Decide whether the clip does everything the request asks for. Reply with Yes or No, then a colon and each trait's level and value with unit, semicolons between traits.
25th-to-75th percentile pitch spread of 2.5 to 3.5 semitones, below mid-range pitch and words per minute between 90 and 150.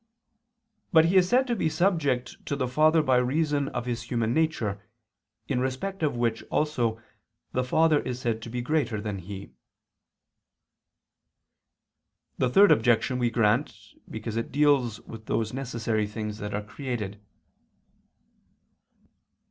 No: average, 5.0 semitones; low, 125 Hz; average, 140 wpm